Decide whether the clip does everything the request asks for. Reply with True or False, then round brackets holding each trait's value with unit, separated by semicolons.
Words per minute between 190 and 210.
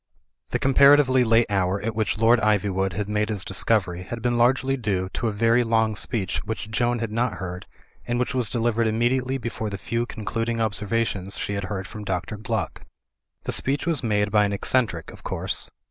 True (195 wpm)